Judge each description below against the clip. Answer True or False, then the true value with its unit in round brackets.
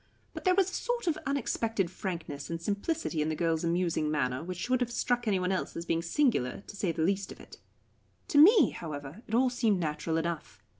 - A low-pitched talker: False (185 Hz)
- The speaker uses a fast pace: True (215 wpm)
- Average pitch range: False (7.0 semitones)